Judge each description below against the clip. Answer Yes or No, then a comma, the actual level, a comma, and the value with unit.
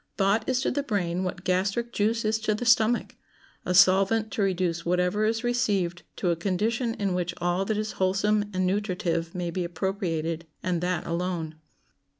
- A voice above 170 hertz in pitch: Yes, high, 190 Hz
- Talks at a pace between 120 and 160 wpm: No, average, 170 wpm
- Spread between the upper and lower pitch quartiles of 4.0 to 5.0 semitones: No, average, 3.4 semitones